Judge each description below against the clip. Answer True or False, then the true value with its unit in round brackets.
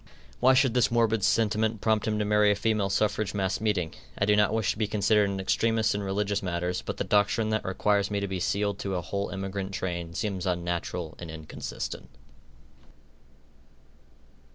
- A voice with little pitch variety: True (2.2 semitones)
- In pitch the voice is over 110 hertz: False (100 Hz)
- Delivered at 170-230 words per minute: True (180 wpm)